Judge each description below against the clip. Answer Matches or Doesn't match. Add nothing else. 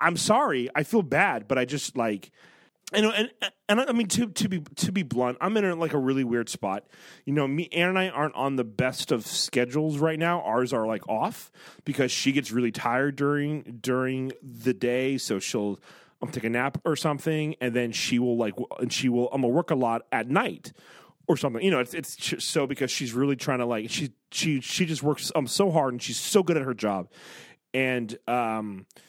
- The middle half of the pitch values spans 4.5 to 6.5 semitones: Matches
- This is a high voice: Doesn't match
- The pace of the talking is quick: Matches